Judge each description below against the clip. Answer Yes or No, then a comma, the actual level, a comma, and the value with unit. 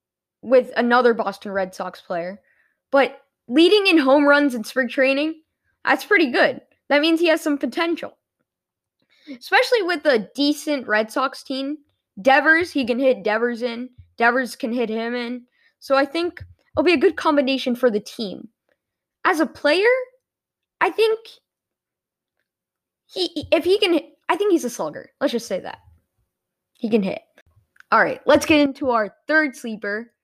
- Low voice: No, very high, 275 Hz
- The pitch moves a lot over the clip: No, average, 4.8 semitones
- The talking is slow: No, average, 160 wpm